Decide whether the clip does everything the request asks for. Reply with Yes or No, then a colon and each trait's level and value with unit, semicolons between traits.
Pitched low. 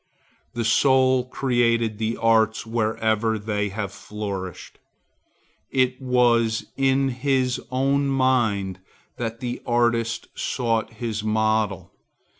Yes: low, 115 Hz